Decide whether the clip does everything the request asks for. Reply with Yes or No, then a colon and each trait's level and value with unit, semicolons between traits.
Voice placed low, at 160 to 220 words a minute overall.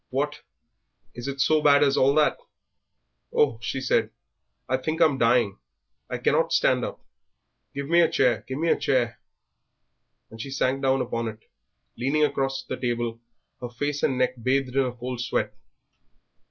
Yes: low, 130 Hz; average, 165 wpm